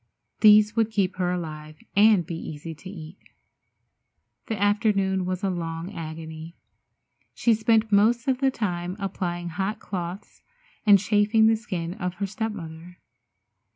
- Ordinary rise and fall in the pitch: Yes, average, 3.7 semitones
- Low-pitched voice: No, high, 190 Hz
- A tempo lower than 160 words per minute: Yes, average, 145 wpm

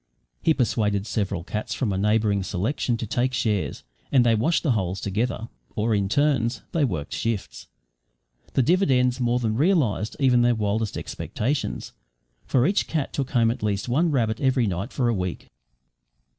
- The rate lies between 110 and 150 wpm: No, average, 170 wpm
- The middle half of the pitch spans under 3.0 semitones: No, average, 3.9 semitones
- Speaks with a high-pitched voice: No, low, 115 Hz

